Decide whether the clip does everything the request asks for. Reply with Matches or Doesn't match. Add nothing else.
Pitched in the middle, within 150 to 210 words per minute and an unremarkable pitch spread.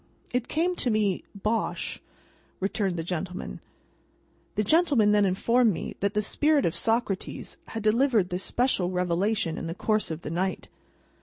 Doesn't match